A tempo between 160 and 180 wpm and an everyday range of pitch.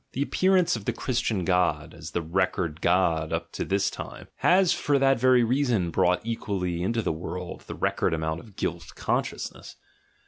No: average, 175 wpm; wide, 6.4 semitones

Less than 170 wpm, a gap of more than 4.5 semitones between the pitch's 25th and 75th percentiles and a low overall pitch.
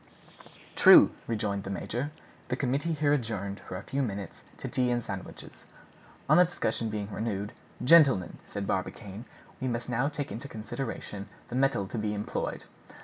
Yes: average, 160 wpm; average, 4.9 semitones; low, 115 Hz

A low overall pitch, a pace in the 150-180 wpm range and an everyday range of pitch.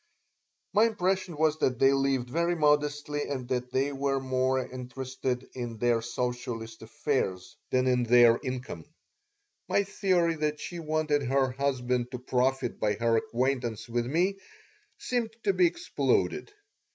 No: low, 130 Hz; average, 140 wpm; average, 3.7 semitones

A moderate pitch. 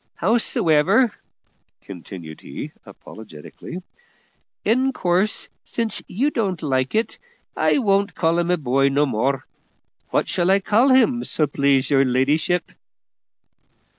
Yes: medium, 170 Hz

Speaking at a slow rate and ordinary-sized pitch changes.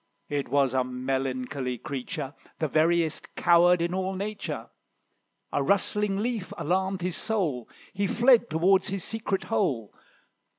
No: slow, 130 wpm; wide, 6.2 semitones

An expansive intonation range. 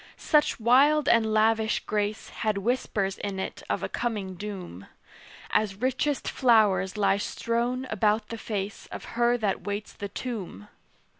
No: average, 3.0 semitones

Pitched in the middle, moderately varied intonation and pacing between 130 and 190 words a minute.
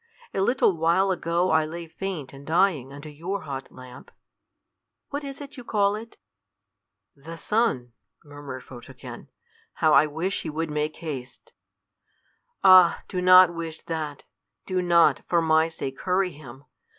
Yes: medium, 165 Hz; average, 4.3 semitones; average, 150 wpm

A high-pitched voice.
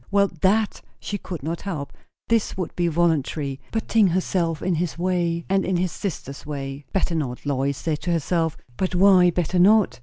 No: medium, 175 Hz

